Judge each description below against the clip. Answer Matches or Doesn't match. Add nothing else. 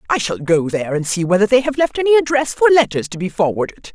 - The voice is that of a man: Doesn't match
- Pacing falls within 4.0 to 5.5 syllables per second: Doesn't match